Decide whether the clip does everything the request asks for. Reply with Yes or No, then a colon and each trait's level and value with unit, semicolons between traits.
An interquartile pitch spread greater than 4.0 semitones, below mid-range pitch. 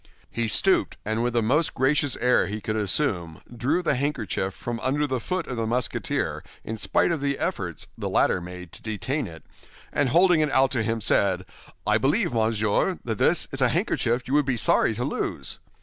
Yes: average, 4.8 semitones; low, 120 Hz